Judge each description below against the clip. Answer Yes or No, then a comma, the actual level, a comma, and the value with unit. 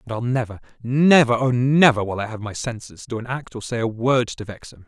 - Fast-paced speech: Yes, fast, 235 wpm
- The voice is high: No, low, 120 Hz